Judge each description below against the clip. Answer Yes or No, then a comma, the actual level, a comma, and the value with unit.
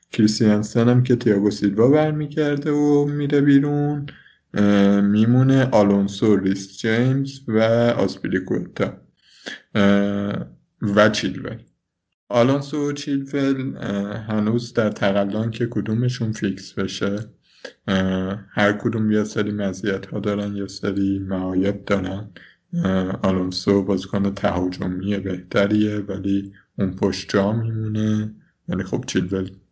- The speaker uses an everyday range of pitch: Yes, average, 3.2 semitones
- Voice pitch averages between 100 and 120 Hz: Yes, low, 105 Hz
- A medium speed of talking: No, slow, 100 wpm